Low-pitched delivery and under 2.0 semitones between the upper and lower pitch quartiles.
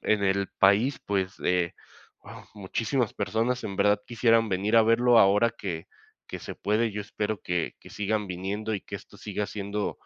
No: low, 105 Hz; narrow, 2.4 semitones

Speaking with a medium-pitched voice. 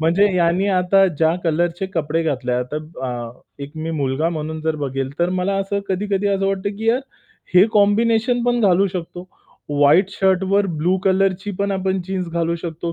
Yes: medium, 180 Hz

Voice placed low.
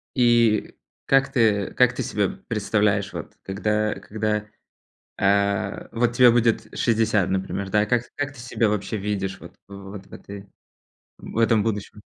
Yes: low, 105 Hz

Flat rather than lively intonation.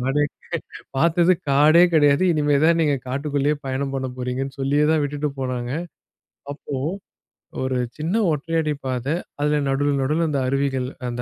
Yes: narrow, 2.2 semitones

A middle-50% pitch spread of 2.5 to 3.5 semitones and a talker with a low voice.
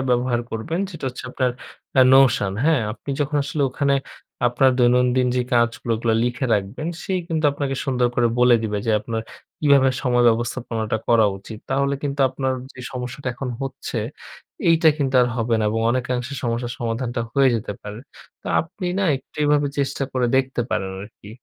Yes: average, 2.8 semitones; low, 125 Hz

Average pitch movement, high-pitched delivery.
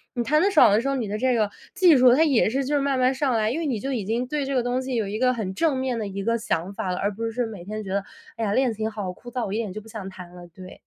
Yes: average, 4.1 semitones; high, 230 Hz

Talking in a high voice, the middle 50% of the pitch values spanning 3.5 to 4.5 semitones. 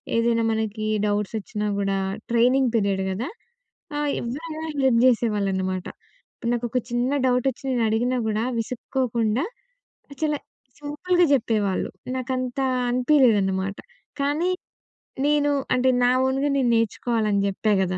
Yes: high, 235 Hz; average, 3.8 semitones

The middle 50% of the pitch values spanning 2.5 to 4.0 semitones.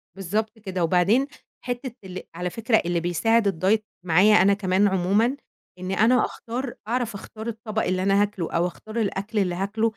Yes: average, 3.4 semitones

